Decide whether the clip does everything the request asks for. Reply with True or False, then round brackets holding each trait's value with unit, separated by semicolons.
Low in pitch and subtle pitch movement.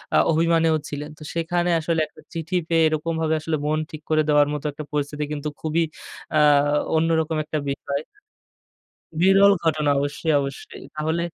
False (155 Hz; 1.7 semitones)